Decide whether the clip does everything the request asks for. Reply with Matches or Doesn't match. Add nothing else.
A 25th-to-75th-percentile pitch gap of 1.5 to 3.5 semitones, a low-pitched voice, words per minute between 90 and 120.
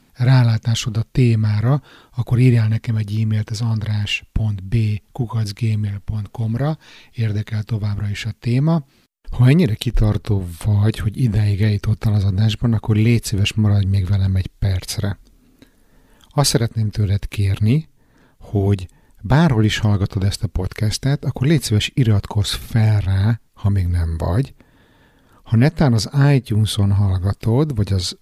Doesn't match